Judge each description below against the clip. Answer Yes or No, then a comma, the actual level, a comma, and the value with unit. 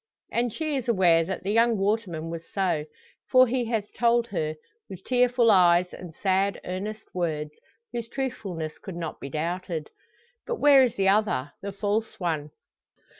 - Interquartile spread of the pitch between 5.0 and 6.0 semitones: Yes, wide, 5.4 semitones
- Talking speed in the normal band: Yes, average, 165 wpm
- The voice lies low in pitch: No, high, 195 Hz